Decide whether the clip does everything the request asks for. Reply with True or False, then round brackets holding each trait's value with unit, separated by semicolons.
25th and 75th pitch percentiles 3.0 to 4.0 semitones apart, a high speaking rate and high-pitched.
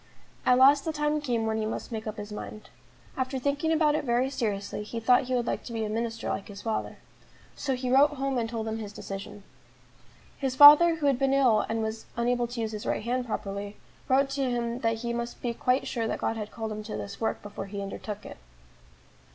True (3.5 semitones; 235 wpm; 235 Hz)